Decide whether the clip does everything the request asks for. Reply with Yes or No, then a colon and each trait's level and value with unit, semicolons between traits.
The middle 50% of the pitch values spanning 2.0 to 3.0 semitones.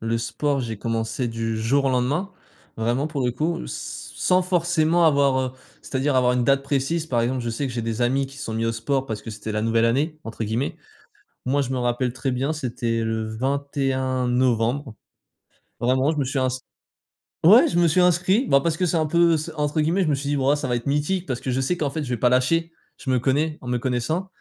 No: average, 4.1 semitones